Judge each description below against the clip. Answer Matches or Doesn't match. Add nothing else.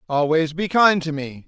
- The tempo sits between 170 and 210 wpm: Matches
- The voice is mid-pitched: Matches